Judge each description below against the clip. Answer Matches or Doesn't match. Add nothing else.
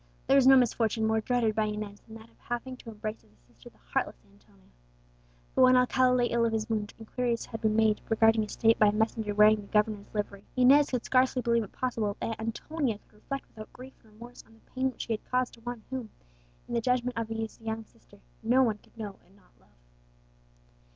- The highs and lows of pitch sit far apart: Doesn't match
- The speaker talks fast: Matches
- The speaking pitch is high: Matches